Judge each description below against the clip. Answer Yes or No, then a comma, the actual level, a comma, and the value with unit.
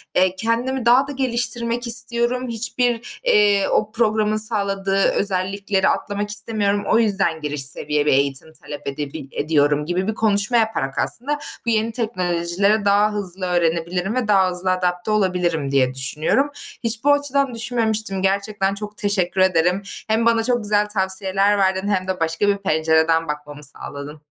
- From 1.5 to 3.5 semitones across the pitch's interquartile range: No, average, 4.3 semitones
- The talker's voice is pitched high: Yes, high, 200 Hz